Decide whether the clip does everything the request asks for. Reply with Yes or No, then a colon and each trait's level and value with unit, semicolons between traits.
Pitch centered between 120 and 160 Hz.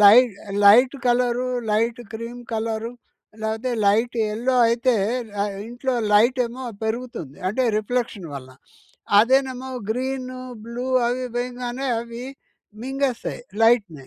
No: high, 240 Hz